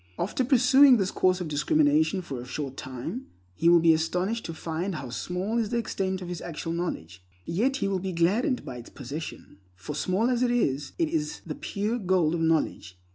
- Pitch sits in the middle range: Yes, medium, 180 Hz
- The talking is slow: No, fast, 205 wpm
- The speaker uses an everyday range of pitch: No, wide, 6.5 semitones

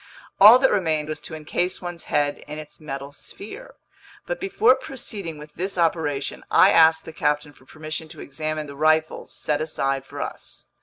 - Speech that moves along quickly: No, average, 175 wpm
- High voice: No, medium, 155 Hz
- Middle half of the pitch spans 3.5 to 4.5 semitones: No, average, 3.1 semitones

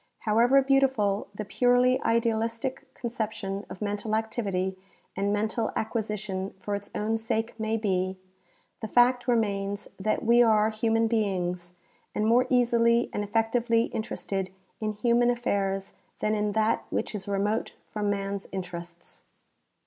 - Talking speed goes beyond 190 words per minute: No, slow, 135 wpm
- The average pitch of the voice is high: Yes, high, 215 Hz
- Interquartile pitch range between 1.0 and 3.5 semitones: Yes, narrow, 2.5 semitones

